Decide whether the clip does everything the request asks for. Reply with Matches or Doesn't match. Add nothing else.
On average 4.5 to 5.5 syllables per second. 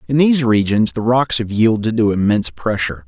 Doesn't match